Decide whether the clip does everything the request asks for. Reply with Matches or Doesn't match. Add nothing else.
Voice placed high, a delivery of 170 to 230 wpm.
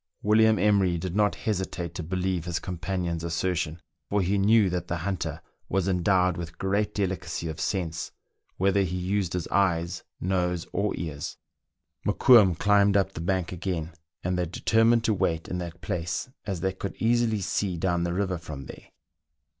Doesn't match